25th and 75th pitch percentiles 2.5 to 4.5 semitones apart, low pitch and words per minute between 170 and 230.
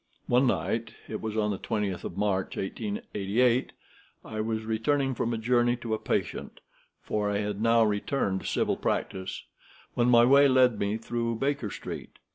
No: average, 2.9 semitones; low, 115 Hz; average, 160 wpm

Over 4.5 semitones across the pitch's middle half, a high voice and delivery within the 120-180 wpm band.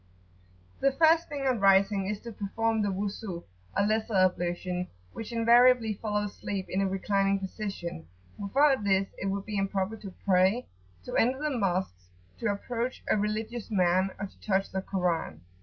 No: average, 2.9 semitones; high, 200 Hz; average, 165 wpm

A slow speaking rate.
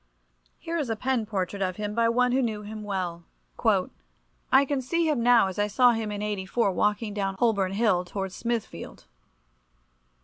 No: average, 175 wpm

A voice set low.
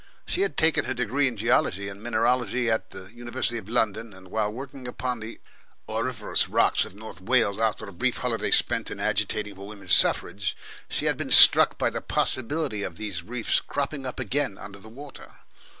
Yes: low, 115 Hz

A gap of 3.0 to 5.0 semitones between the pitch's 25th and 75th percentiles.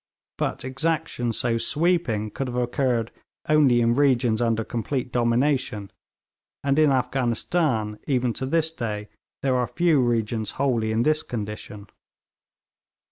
Yes: average, 3.5 semitones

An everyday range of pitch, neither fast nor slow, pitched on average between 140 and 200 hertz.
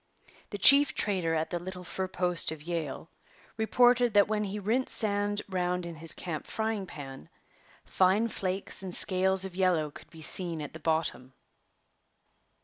Yes: average, 3.7 semitones; average, 160 wpm; medium, 185 Hz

